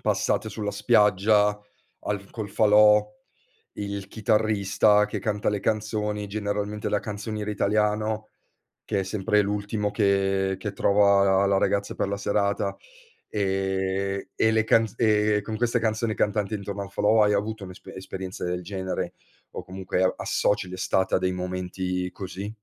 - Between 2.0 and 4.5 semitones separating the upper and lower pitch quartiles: No, narrow, 1.6 semitones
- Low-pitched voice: Yes, low, 100 Hz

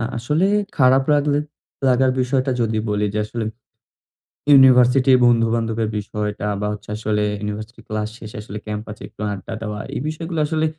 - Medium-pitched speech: No, low, 115 Hz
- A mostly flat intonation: No, average, 3.8 semitones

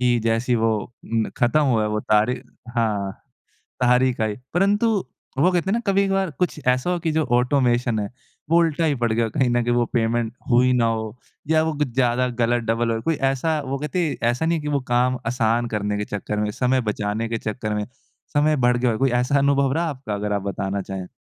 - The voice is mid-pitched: No, low, 125 Hz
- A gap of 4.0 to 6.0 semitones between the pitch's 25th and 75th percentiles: Yes, average, 4.4 semitones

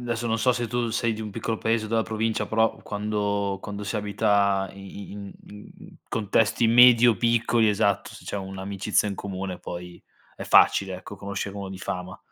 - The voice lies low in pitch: Yes, low, 105 Hz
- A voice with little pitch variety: Yes, narrow, 2.3 semitones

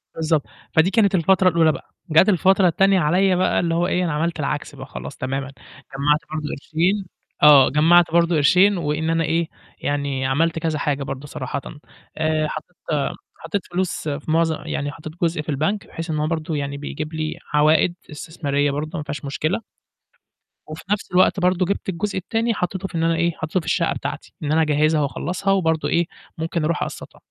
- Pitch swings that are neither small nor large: Yes, average, 3.0 semitones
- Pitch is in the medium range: Yes, medium, 160 Hz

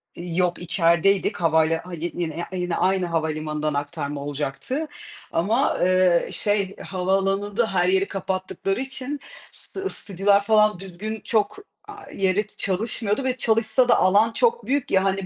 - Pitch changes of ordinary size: Yes, average, 4.0 semitones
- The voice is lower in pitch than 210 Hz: Yes, high, 190 Hz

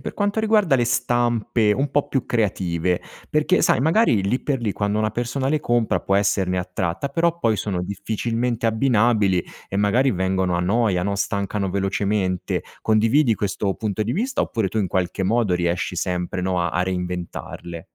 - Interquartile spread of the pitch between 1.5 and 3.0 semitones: No, average, 4.5 semitones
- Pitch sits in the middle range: No, low, 105 Hz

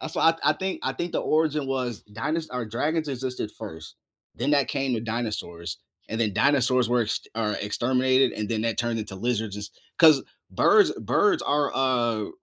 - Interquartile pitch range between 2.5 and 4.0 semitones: No, average, 4.4 semitones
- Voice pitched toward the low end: Yes, low, 125 Hz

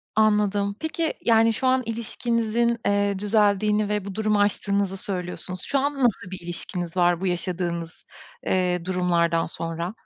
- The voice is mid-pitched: No, high, 200 Hz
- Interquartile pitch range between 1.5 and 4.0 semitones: Yes, average, 3.5 semitones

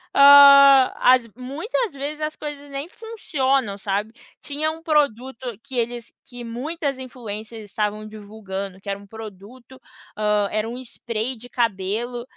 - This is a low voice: No, high, 245 Hz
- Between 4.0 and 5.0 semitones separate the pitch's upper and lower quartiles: Yes, average, 4.7 semitones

